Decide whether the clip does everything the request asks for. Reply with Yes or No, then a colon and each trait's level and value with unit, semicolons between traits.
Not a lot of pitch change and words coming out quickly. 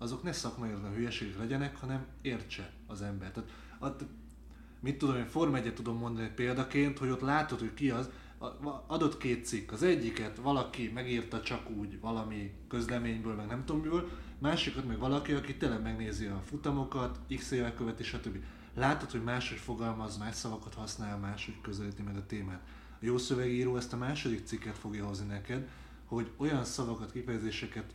No: average, 3.3 semitones; fast, 165 wpm